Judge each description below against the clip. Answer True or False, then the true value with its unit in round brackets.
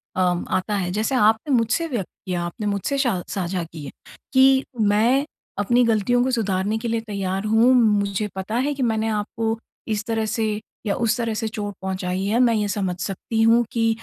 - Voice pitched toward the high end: True (215 Hz)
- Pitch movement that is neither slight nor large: True (3.0 semitones)